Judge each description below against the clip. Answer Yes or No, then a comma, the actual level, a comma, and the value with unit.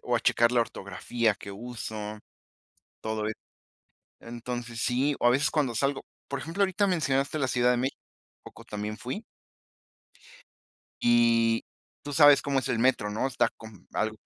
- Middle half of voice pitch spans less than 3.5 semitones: No, average, 3.8 semitones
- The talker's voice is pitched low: Yes, low, 120 Hz